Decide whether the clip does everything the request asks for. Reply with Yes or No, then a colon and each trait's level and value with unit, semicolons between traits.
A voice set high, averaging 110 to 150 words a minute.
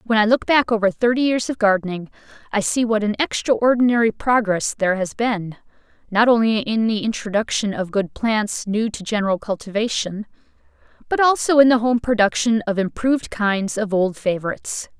No: high, 220 Hz; average, 170 wpm